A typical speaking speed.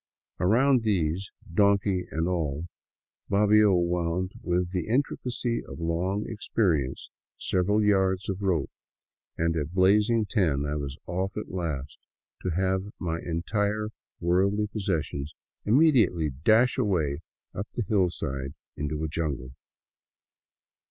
No: slow, 120 wpm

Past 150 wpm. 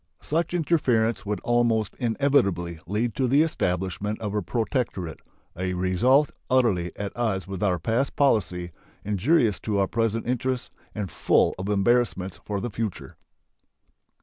No: average, 140 wpm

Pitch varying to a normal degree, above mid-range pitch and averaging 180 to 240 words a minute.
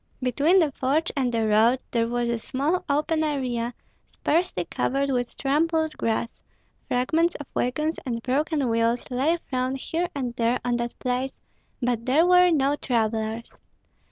No: average, 4.3 semitones; very high, 260 Hz; average, 155 wpm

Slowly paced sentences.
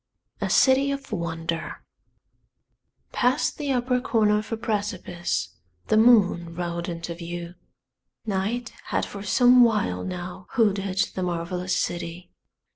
Yes: slow, 120 wpm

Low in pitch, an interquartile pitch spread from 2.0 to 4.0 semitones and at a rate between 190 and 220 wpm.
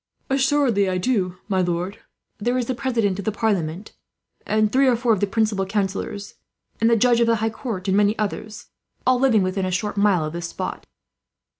No: high, 210 Hz; average, 3.5 semitones; average, 200 wpm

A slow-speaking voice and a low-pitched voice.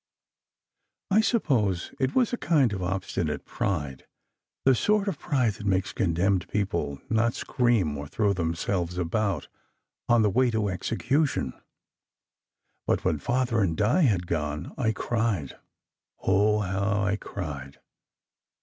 Yes: slow, 130 wpm; low, 100 Hz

